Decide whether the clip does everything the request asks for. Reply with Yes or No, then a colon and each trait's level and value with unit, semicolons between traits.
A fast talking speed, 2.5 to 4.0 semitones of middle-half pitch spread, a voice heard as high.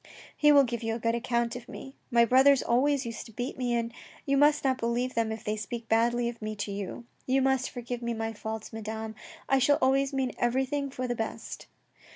Yes: fast, 215 wpm; average, 2.8 semitones; high, 240 Hz